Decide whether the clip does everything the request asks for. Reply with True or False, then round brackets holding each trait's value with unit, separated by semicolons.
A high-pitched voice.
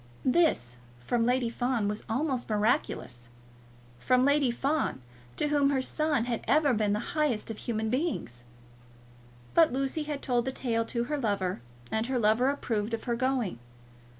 True (245 Hz)